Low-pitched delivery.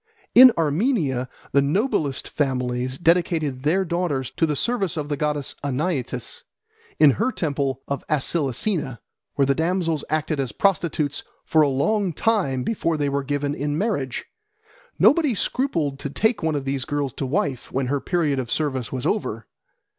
No: medium, 145 Hz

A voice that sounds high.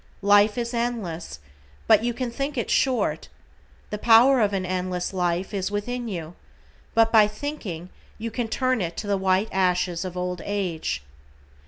Yes: high, 205 Hz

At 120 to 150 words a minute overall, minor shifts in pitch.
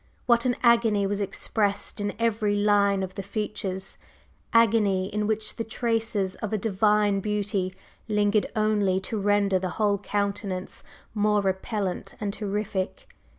Yes: average, 140 wpm; narrow, 1.5 semitones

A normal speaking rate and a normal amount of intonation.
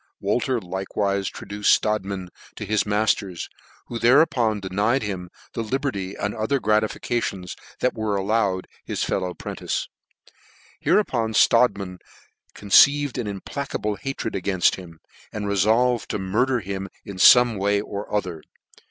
No: slow, 130 wpm; average, 3.3 semitones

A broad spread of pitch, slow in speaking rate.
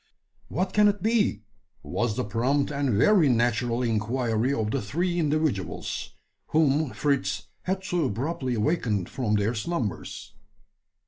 Yes: wide, 6.3 semitones; slow, 130 wpm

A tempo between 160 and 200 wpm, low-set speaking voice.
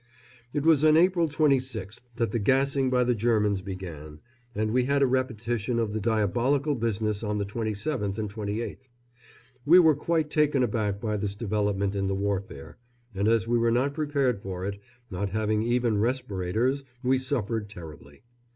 Yes: average, 170 wpm; low, 115 Hz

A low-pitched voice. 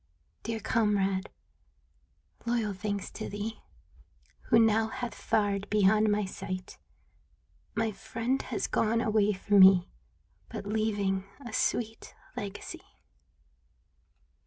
No: high, 210 Hz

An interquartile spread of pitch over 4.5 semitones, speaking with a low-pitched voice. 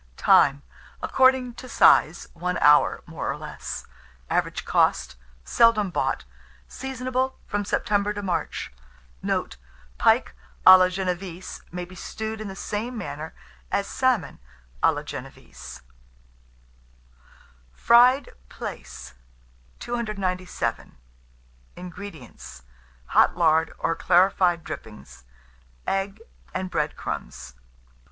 No: average, 4.9 semitones; medium, 185 Hz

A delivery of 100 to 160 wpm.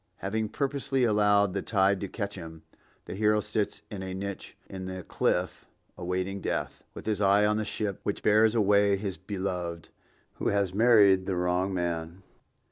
No: average, 170 wpm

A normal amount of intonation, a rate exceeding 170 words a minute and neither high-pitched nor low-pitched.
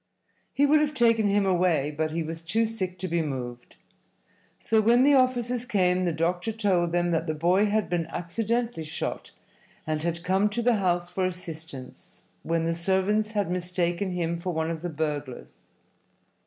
Yes: average, 4.4 semitones; average, 180 wpm; medium, 180 Hz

